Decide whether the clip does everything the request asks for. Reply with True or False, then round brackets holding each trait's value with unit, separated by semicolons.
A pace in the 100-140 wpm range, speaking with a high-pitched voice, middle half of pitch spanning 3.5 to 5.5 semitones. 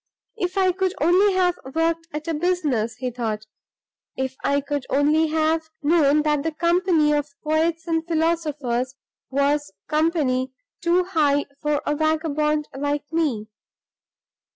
False (135 wpm; 305 Hz; 2.7 semitones)